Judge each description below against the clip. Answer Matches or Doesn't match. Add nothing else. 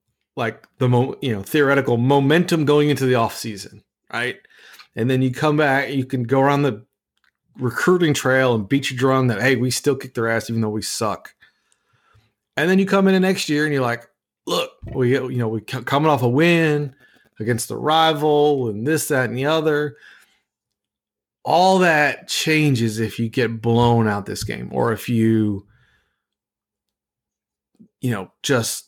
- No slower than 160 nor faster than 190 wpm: Matches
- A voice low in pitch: Matches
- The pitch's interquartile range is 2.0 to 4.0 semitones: Doesn't match